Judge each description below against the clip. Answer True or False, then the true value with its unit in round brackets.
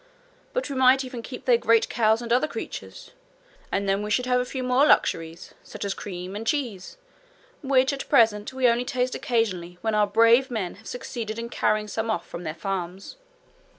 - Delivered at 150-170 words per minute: False (195 wpm)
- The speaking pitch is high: True (230 Hz)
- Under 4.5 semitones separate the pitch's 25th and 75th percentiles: True (3.8 semitones)